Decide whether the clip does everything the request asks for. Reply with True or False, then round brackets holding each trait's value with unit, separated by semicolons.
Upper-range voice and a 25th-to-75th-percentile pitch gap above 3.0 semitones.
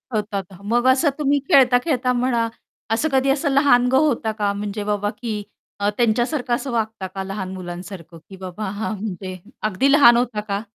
True (225 Hz; 4.2 semitones)